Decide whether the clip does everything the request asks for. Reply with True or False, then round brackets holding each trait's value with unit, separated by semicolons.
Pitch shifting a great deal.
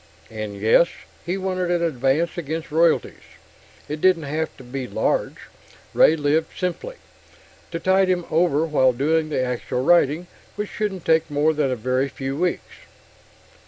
False (4.4 semitones)